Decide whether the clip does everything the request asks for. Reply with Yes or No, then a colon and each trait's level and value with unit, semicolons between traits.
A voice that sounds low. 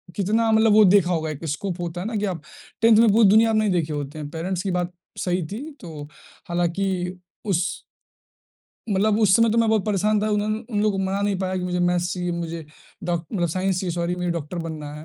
No: medium, 185 Hz